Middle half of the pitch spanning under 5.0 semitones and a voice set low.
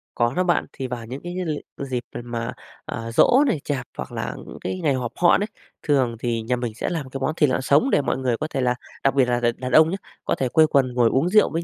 Yes: average, 4.3 semitones; low, 130 Hz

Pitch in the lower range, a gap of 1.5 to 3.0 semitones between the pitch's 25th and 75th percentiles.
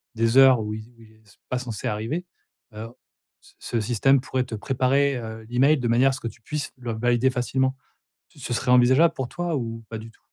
Yes: low, 125 Hz; average, 2.7 semitones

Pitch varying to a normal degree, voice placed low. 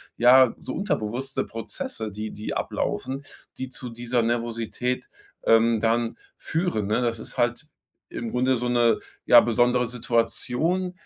No: narrow, 1.9 semitones; low, 120 Hz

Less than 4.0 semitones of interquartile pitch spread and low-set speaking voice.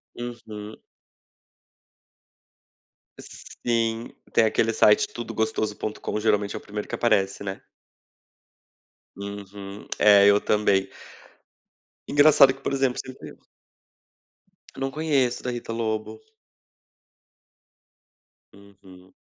Yes: average, 3.0 semitones; low, 110 Hz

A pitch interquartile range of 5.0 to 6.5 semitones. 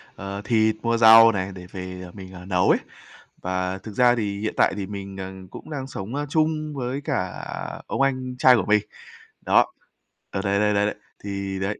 No: average, 4.2 semitones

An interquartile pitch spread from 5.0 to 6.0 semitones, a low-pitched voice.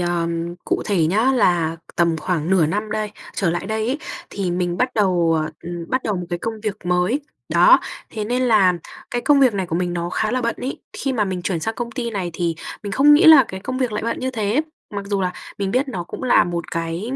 No: average, 5.3 semitones; high, 200 Hz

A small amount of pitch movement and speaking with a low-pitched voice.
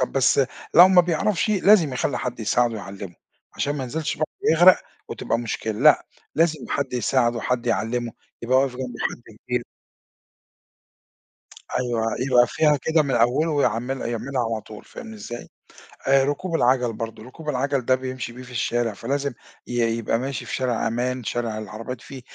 No: average, 3.3 semitones; low, 125 Hz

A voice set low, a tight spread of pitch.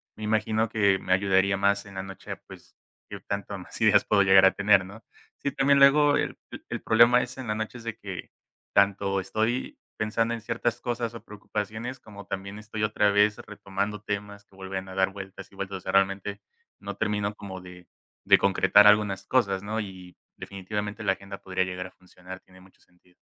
Yes: low, 100 Hz; narrow, 2.0 semitones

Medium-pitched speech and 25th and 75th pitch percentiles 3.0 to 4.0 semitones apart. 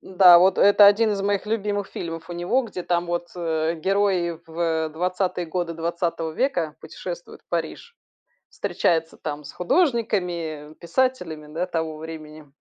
Yes: medium, 175 Hz; average, 3.5 semitones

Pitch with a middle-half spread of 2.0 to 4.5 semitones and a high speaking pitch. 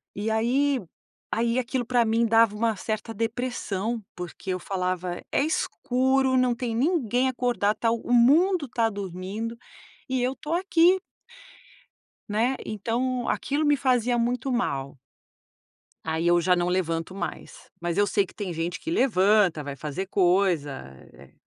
No: wide, 5.4 semitones; high, 225 Hz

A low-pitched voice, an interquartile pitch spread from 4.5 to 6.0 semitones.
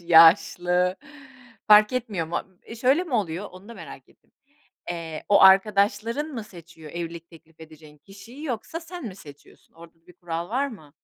No: medium, 185 Hz; wide, 5.5 semitones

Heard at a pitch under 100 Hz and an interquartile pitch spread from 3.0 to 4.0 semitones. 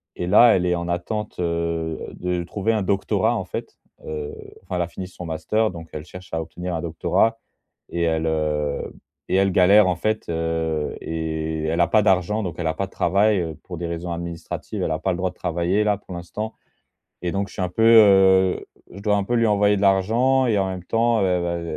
Yes: very low, 90 Hz; average, 3.4 semitones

